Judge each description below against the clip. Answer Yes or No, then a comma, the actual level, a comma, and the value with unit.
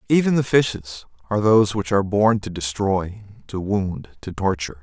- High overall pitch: No, low, 100 Hz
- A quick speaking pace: No, average, 175 wpm